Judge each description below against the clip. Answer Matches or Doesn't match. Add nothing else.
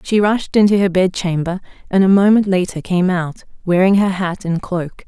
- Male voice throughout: Doesn't match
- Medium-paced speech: Matches